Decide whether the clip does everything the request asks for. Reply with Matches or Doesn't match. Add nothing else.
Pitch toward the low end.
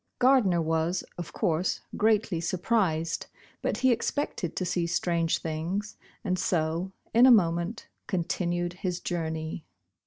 Doesn't match